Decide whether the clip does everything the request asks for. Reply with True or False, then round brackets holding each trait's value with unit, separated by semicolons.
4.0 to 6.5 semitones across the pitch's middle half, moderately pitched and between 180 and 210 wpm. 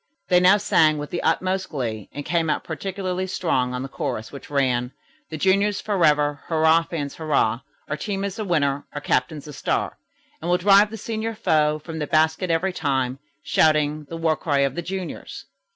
True (4.3 semitones; 160 Hz; 190 wpm)